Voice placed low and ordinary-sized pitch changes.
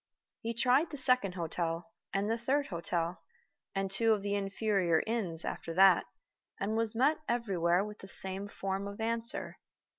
No: high, 200 Hz; average, 3.6 semitones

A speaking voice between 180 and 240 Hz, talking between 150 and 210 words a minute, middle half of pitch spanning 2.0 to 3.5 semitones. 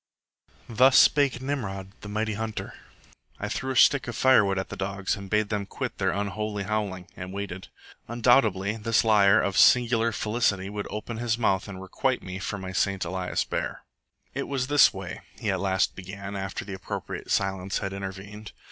No: low, 100 Hz; average, 180 wpm; average, 2.8 semitones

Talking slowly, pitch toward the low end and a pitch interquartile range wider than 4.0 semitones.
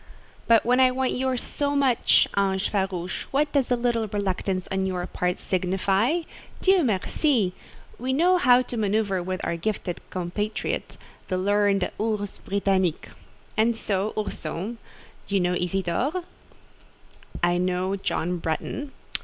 No: slow, 130 wpm; high, 200 Hz; average, 4.9 semitones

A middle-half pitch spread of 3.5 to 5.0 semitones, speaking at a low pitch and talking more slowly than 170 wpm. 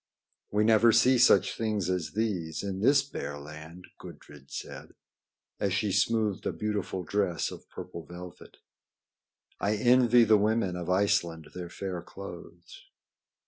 Yes: average, 3.8 semitones; low, 100 Hz; average, 140 wpm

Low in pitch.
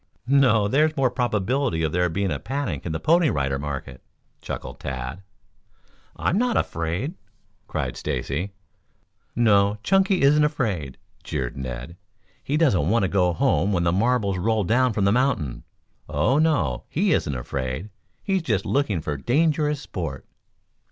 Yes: low, 100 Hz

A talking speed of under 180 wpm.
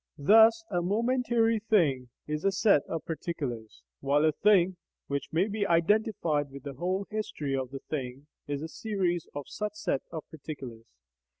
Yes: average, 165 wpm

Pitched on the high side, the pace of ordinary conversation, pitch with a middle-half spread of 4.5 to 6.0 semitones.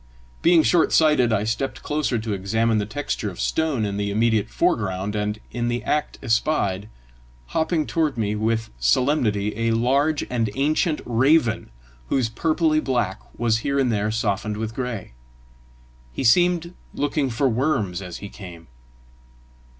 No: low, 115 Hz; average, 150 wpm; wide, 5.6 semitones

